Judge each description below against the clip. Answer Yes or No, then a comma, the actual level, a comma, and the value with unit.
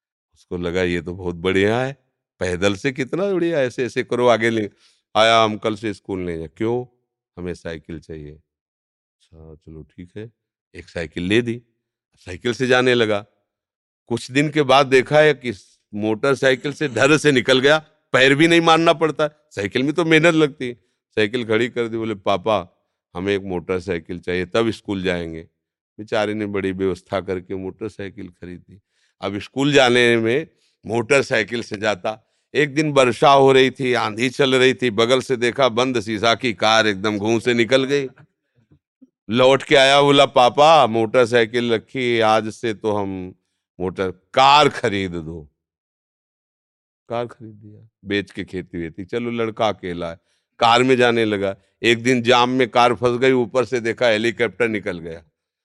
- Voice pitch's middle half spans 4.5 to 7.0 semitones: Yes, average, 5.1 semitones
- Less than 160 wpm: No, average, 170 wpm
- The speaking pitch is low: Yes, low, 115 Hz